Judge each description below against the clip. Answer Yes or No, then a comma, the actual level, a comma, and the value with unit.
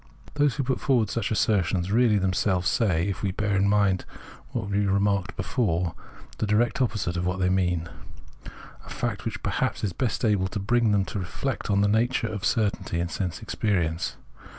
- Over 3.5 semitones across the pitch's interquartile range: No, average, 3.1 semitones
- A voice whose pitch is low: Yes, low, 100 Hz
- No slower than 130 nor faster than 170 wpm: No, average, 195 wpm